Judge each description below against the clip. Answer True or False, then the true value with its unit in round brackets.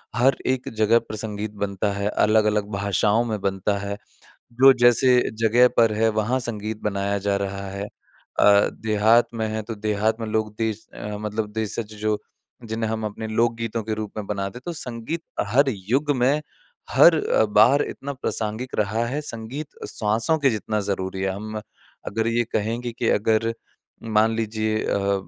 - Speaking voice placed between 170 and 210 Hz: False (110 Hz)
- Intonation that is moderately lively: False (2.0 semitones)